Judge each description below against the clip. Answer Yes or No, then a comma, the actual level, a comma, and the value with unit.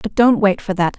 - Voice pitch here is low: No, high, 205 Hz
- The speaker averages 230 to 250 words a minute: No, fast, 305 wpm